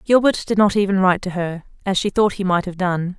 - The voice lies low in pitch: No, high, 190 Hz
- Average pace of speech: No, fast, 265 wpm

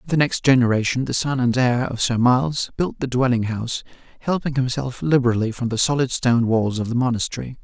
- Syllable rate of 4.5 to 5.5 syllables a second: No, 6.0 syllables/s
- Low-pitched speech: Yes, low, 125 Hz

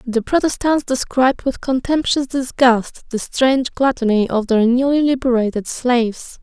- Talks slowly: Yes, slow, 130 wpm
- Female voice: Yes, female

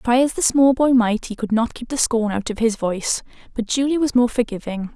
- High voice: Yes, high, 240 Hz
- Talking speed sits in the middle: No, fast, 255 wpm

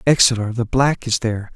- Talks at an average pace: Yes, average, 195 wpm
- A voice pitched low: Yes, low, 120 Hz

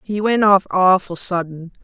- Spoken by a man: No, female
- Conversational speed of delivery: Yes, average, 165 wpm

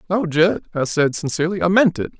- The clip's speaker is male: Yes, male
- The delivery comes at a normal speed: No, fast, 220 wpm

